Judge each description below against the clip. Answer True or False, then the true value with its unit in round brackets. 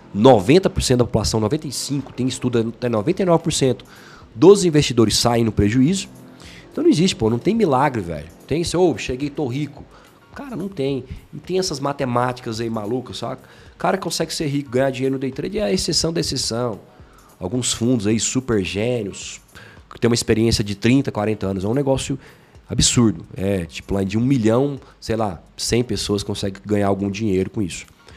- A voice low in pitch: True (120 Hz)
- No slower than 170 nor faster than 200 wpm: True (180 wpm)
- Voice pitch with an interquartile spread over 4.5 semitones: True (5.2 semitones)